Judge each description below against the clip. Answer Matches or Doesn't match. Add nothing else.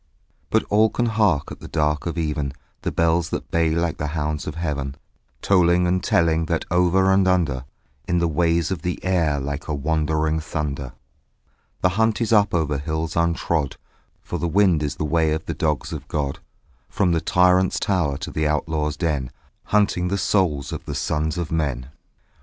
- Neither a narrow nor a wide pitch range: Matches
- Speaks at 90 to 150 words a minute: Doesn't match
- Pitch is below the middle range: Matches